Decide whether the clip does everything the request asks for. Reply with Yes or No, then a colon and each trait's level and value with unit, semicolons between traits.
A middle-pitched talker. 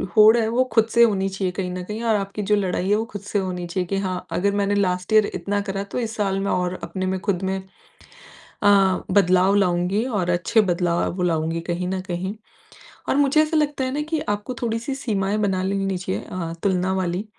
No: high, 195 Hz